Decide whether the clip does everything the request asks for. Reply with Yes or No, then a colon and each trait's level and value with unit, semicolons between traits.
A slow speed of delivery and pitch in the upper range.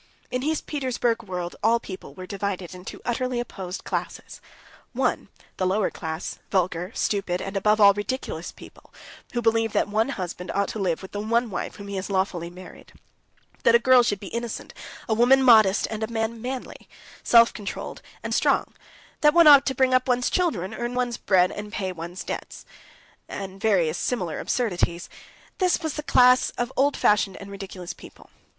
No: average, 180 wpm; high, 210 Hz